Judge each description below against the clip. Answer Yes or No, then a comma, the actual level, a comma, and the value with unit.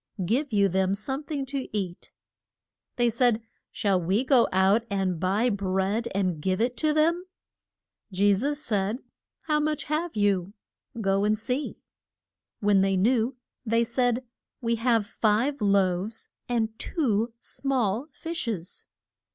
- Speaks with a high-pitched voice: Yes, high, 220 Hz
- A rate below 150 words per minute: Yes, average, 140 wpm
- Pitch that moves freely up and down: No, average, 4.7 semitones